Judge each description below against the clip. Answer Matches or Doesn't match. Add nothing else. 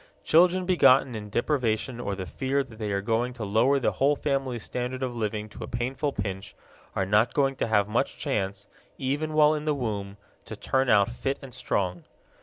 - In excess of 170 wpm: Matches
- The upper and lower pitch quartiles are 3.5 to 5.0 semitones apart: Matches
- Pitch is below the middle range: Matches